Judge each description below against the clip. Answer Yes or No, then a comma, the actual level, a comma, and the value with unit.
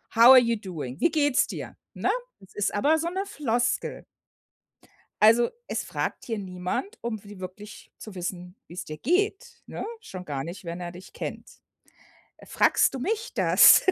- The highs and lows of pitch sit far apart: Yes, wide, 8.1 semitones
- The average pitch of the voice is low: No, high, 215 Hz